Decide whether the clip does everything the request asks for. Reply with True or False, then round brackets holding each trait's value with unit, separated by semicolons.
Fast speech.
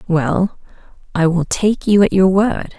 False (170 wpm)